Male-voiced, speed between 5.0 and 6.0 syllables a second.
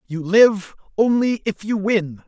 No: male; 3.8 syllables/s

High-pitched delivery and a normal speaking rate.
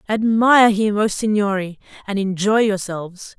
No: high, 205 Hz; slow, 125 wpm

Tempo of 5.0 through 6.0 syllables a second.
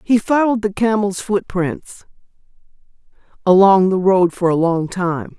No: 4.4 syllables/s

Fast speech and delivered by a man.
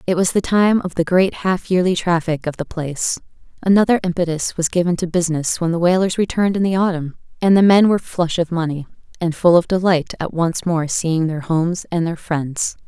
No: fast, 215 wpm; female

